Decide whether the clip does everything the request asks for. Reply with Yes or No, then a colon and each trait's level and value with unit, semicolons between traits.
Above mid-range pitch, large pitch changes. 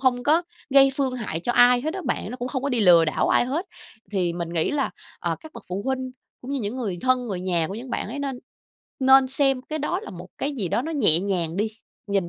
Yes: high, 245 Hz; wide, 6.2 semitones